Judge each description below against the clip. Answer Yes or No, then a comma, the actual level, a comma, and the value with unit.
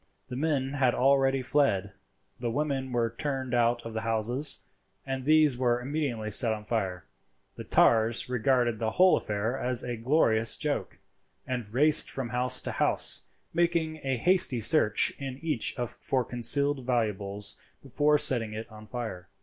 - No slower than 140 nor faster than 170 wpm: Yes, average, 155 wpm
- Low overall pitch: Yes, low, 125 Hz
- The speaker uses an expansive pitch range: No, average, 3.6 semitones